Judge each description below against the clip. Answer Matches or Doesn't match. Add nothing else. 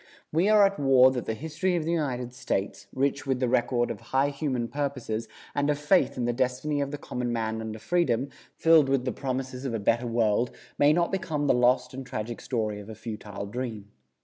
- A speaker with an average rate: Doesn't match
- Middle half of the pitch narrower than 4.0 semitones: Matches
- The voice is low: Matches